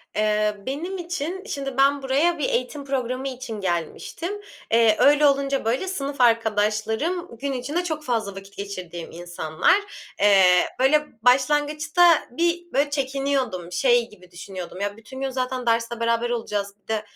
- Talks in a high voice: Yes, very high, 255 Hz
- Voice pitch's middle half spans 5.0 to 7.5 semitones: Yes, average, 5.3 semitones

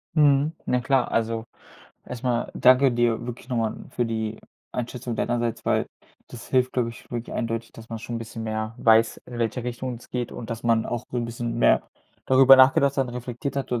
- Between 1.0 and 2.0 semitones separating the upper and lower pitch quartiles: Yes, narrow, 1.7 semitones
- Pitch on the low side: Yes, low, 120 Hz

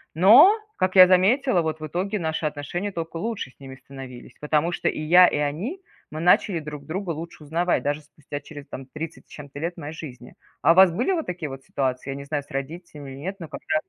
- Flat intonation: No, average, 3.8 semitones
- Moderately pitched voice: Yes, medium, 160 Hz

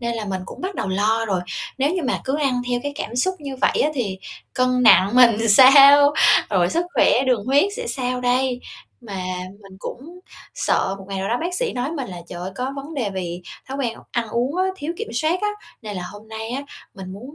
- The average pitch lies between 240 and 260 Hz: Yes, very high, 250 Hz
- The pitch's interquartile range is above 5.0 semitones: Yes, wide, 5.4 semitones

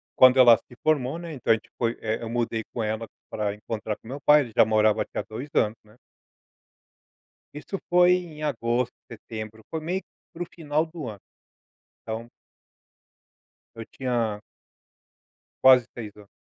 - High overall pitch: No, low, 120 Hz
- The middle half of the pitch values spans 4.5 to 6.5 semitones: Yes, average, 5.1 semitones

